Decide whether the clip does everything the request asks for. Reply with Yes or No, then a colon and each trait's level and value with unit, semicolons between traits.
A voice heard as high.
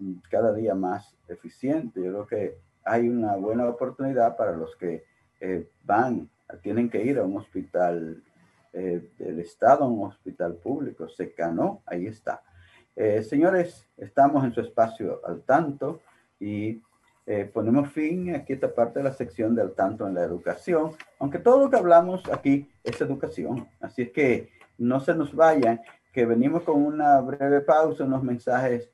No: low, 120 Hz